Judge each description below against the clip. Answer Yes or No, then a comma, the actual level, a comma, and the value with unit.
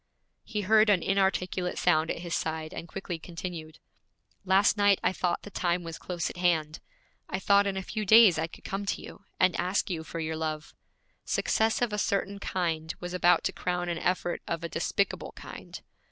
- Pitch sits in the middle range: Yes, medium, 180 Hz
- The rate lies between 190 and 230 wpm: Yes, average, 195 wpm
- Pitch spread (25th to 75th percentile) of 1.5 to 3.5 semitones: Yes, average, 2.9 semitones